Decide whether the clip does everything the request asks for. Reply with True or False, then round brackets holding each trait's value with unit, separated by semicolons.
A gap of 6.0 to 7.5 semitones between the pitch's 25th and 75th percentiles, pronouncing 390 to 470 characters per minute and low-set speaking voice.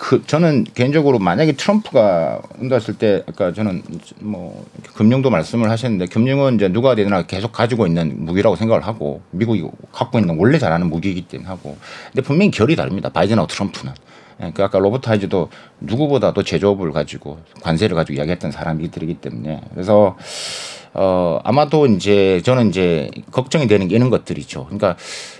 True (6.4 semitones; 410 characters per minute; 100 Hz)